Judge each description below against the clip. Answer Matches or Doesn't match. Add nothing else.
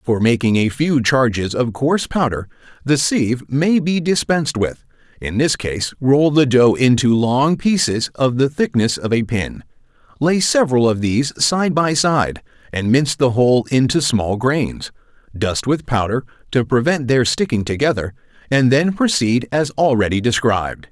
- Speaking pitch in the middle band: Doesn't match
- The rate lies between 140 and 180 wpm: Matches